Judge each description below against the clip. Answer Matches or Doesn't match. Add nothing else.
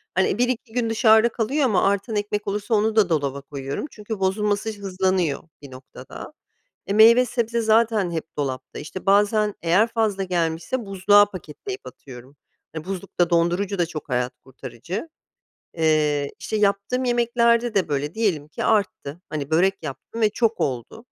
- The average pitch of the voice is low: Doesn't match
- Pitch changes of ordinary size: Doesn't match